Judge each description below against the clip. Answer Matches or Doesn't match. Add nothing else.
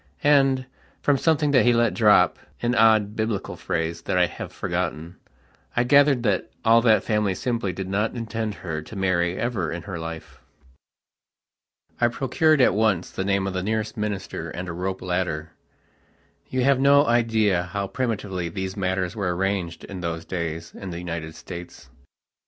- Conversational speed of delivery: Matches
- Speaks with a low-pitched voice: Matches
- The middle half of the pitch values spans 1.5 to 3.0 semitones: Doesn't match